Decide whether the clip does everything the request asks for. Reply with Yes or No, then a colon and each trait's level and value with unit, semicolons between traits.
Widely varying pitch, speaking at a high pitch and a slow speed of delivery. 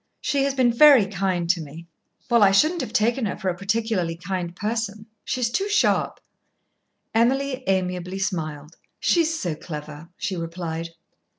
No: wide, 5.8 semitones; high, 195 Hz; average, 155 wpm